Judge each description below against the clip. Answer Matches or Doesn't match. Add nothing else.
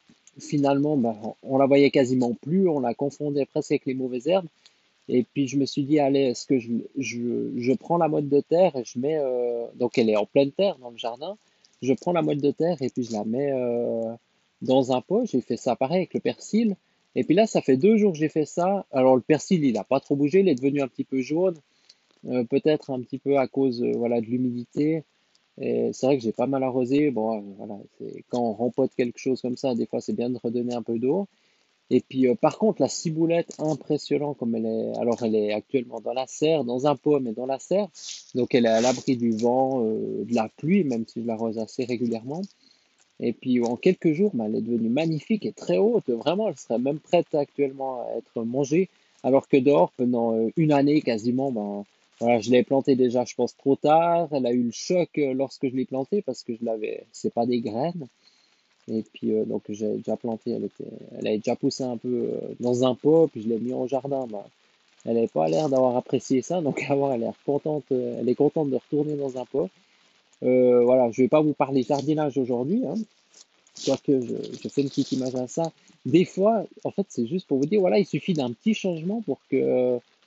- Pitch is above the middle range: Doesn't match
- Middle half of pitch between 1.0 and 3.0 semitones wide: Doesn't match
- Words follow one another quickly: Matches